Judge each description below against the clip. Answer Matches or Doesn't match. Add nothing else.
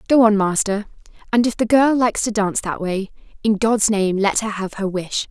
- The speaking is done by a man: Doesn't match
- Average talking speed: Doesn't match